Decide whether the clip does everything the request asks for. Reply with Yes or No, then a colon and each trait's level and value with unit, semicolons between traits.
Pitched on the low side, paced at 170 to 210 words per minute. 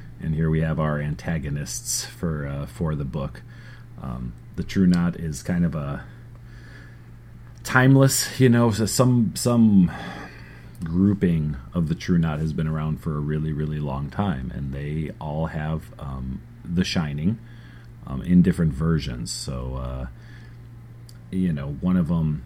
No: very low, 85 Hz; average, 150 wpm